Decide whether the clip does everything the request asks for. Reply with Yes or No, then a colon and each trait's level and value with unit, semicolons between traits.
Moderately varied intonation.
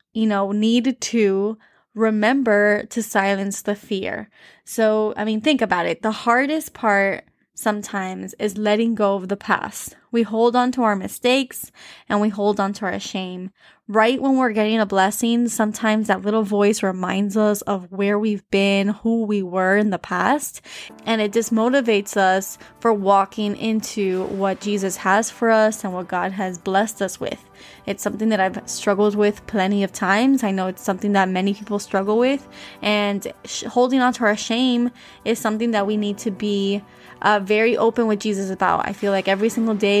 No: narrow, 2.2 semitones